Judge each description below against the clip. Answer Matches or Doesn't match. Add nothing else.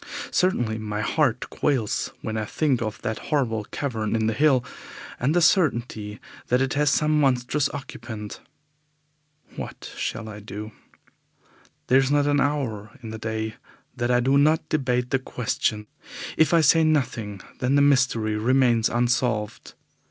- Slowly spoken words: Doesn't match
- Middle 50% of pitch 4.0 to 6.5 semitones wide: Matches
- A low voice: Matches